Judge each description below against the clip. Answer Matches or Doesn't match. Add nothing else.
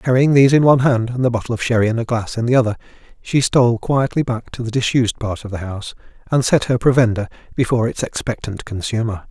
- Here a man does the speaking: Matches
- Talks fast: Matches